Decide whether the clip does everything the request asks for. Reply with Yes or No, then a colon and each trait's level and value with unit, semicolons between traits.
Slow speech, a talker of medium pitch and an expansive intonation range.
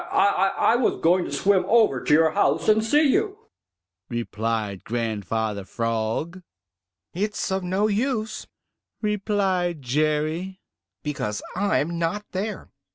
Yes: slow, 120 wpm; medium, 180 Hz; wide, 8.9 semitones